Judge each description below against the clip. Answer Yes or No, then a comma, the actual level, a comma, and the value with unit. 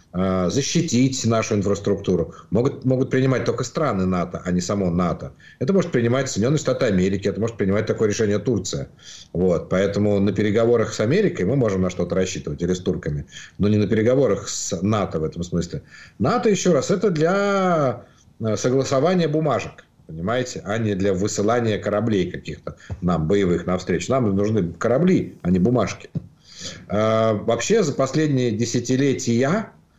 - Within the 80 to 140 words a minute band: No, average, 150 wpm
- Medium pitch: No, low, 110 Hz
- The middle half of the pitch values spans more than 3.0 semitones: Yes, average, 4.8 semitones